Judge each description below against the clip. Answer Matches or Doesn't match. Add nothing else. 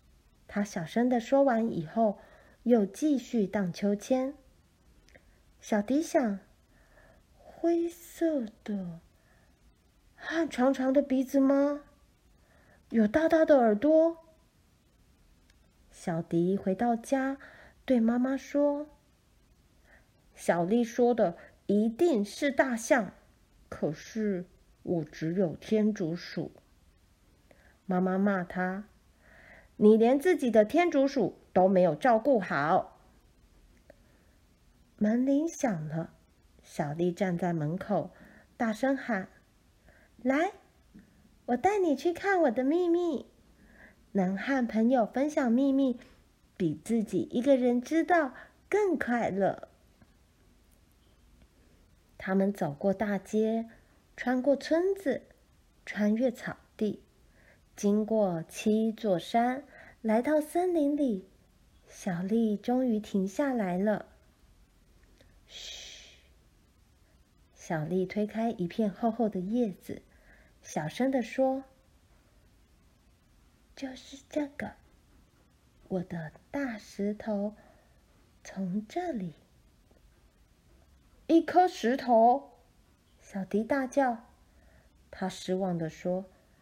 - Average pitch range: Doesn't match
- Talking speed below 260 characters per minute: Matches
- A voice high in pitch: Matches